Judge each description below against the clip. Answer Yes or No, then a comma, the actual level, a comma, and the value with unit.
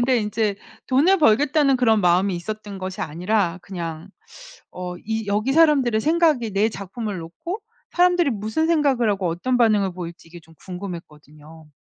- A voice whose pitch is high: Yes, high, 210 Hz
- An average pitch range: No, wide, 6.3 semitones